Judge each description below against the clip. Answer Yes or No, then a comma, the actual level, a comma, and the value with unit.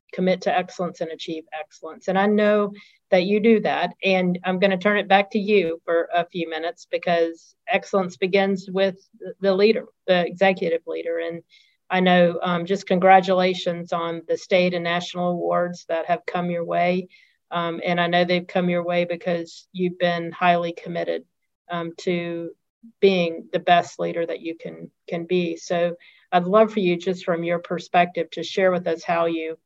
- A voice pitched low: No, medium, 180 Hz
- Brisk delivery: No, average, 185 wpm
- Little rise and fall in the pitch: Yes, narrow, 2.0 semitones